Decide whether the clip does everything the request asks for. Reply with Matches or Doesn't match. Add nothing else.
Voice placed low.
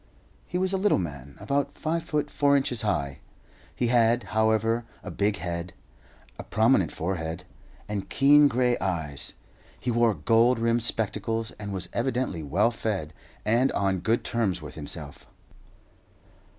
Matches